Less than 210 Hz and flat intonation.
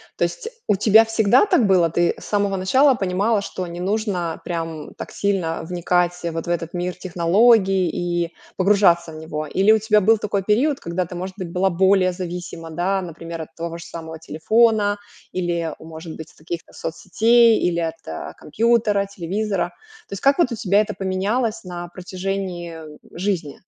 No: medium, 185 Hz; average, 3.3 semitones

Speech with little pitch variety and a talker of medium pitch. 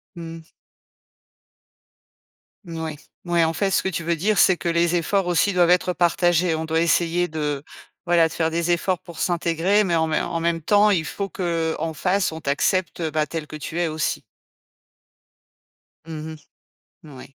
Yes: narrow, 1.7 semitones; medium, 170 Hz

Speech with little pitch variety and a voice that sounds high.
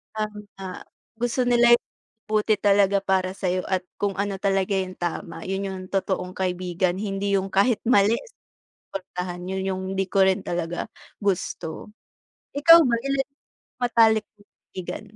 Yes: narrow, 2.3 semitones; high, 195 Hz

